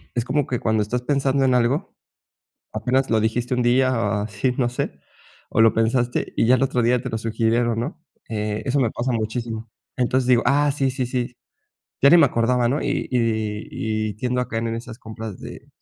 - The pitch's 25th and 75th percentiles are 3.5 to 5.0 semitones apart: No, narrow, 2.4 semitones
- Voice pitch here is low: Yes, low, 120 Hz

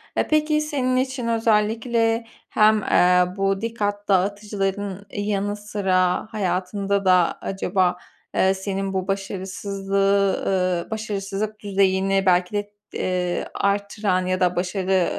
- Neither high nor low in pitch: No, high, 200 Hz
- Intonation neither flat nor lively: No, narrow, 2.0 semitones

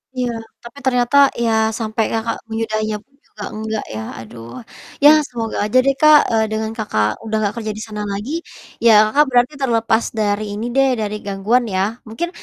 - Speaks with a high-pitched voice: Yes, high, 220 Hz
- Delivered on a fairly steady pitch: Yes, narrow, 2.3 semitones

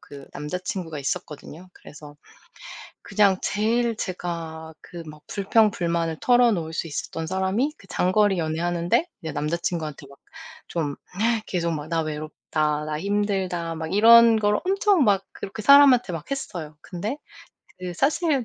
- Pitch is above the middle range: No, medium, 180 Hz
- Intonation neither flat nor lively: Yes, average, 4.8 semitones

